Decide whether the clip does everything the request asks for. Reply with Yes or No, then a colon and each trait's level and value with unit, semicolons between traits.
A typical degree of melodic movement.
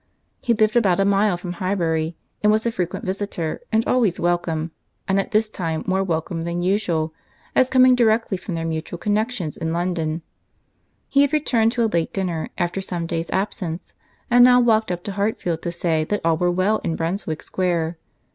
Yes: average, 4.4 semitones